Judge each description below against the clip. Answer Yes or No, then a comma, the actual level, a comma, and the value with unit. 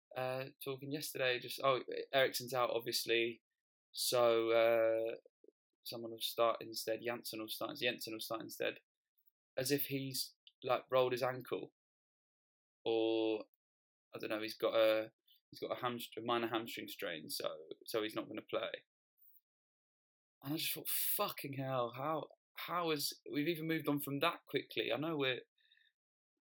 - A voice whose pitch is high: No, low, 130 Hz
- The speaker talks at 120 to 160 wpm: Yes, average, 155 wpm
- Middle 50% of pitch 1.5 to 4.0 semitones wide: No, wide, 5.6 semitones